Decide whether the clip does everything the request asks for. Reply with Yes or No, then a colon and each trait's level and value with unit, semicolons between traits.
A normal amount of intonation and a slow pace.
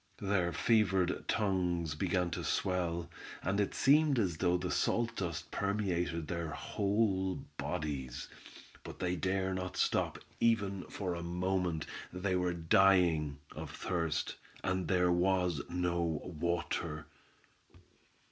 No: narrow, 2.1 semitones; slow, 120 wpm